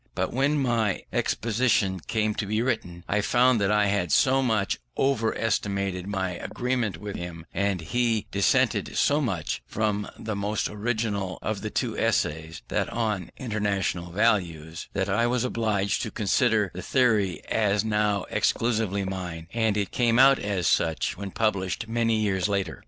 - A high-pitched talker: No, low, 105 Hz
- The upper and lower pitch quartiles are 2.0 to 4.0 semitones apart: Yes, average, 3.1 semitones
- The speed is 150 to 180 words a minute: Yes, average, 160 wpm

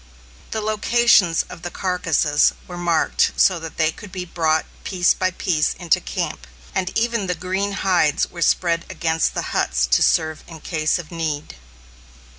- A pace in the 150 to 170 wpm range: Yes, average, 165 wpm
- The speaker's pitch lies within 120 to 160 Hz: No, medium, 175 Hz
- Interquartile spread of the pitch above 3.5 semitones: No, average, 2.8 semitones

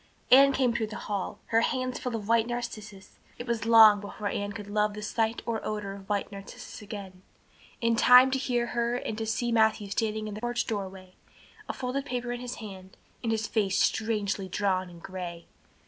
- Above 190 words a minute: Yes, average, 200 wpm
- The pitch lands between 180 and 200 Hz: No, high, 220 Hz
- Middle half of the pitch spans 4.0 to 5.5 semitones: No, average, 2.9 semitones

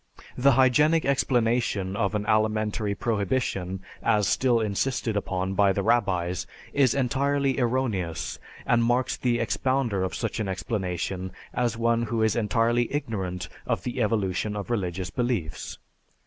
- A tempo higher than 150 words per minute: No, slow, 135 wpm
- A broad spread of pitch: No, average, 4.1 semitones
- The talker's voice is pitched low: Yes, low, 115 Hz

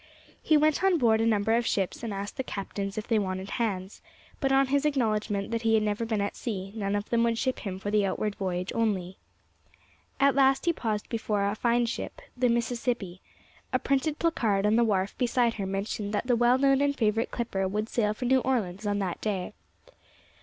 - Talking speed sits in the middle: No, fast, 210 wpm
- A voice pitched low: No, high, 220 Hz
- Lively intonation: No, average, 3.5 semitones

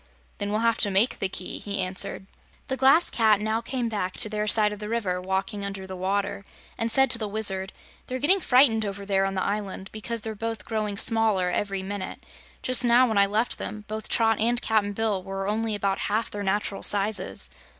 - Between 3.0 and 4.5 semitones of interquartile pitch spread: No, narrow, 2.4 semitones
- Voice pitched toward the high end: Yes, high, 210 Hz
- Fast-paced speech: Yes, fast, 210 wpm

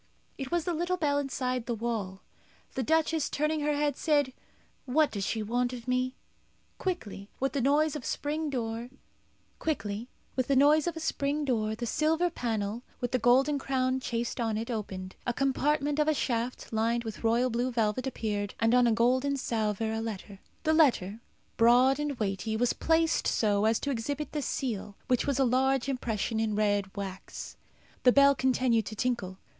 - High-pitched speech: Yes, very high, 250 Hz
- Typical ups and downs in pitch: Yes, average, 4.2 semitones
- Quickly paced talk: No, average, 170 wpm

